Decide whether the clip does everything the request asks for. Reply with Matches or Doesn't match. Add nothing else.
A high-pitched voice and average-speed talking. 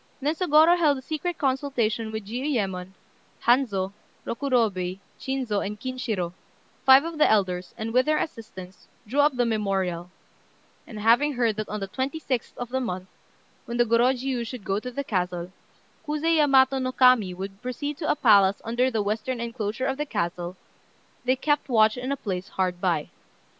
Matches